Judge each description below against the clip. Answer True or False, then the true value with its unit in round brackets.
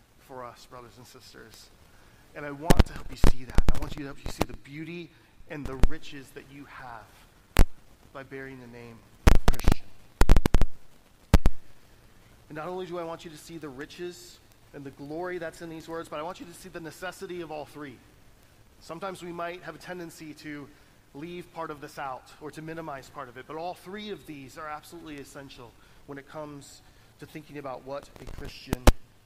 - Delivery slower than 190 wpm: False (205 wpm)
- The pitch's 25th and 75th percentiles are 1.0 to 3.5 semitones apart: False (5.4 semitones)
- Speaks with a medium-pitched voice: True (145 Hz)